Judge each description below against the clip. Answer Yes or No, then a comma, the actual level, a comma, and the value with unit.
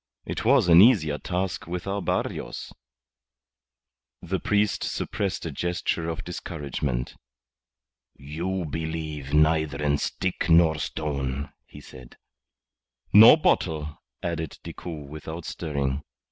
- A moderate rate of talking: No, slow, 110 wpm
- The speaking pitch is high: No, very low, 80 Hz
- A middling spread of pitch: Yes, average, 3.3 semitones